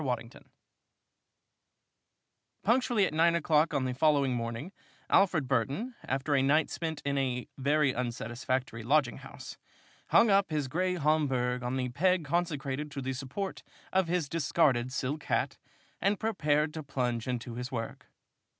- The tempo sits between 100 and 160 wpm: Yes, average, 145 wpm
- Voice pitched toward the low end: No, medium, 145 Hz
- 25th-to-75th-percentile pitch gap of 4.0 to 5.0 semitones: Yes, average, 4.4 semitones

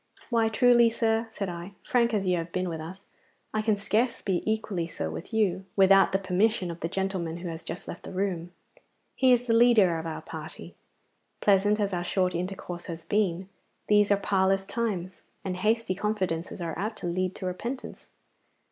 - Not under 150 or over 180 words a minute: No, average, 190 wpm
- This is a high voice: Yes, high, 195 Hz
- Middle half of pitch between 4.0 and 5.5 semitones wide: No, average, 3.5 semitones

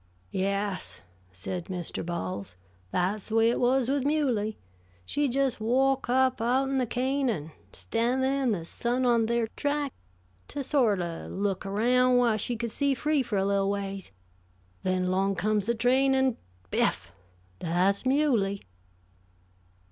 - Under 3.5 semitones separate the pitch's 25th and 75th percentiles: No, average, 5.0 semitones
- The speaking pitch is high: Yes, high, 230 Hz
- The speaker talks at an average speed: Yes, average, 155 wpm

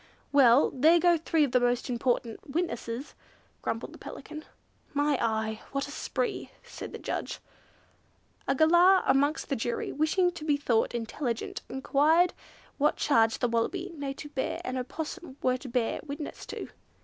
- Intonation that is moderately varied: Yes, average, 4.3 semitones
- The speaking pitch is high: Yes, very high, 280 Hz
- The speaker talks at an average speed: Yes, average, 155 wpm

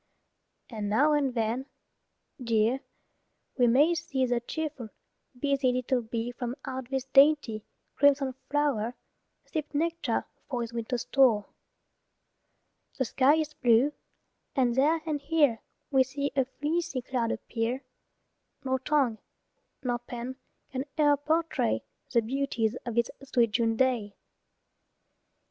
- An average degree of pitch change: Yes, average, 3.3 semitones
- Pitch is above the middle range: Yes, very high, 260 Hz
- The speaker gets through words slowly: Yes, slow, 125 wpm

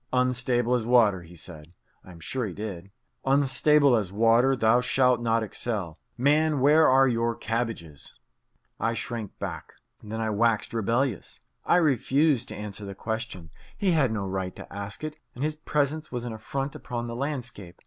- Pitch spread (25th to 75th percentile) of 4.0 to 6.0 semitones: Yes, average, 4.3 semitones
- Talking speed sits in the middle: Yes, average, 170 wpm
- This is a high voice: No, low, 120 Hz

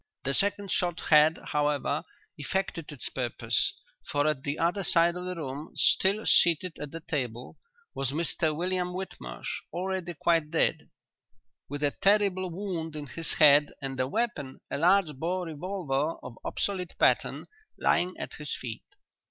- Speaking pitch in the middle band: Yes, medium, 165 Hz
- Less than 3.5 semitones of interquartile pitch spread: No, average, 4.0 semitones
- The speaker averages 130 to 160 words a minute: Yes, average, 150 wpm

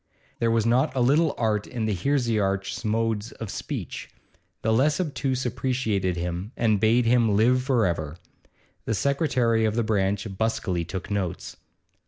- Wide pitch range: No, average, 3.7 semitones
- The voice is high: No, low, 115 Hz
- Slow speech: No, average, 155 wpm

